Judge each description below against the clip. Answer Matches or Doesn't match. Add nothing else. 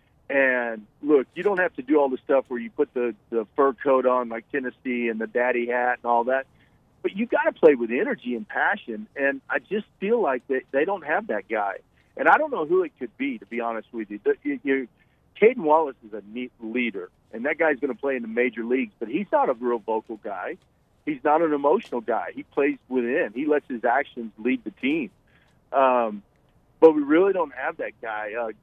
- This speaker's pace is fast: Matches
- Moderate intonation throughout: Matches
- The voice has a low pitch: Matches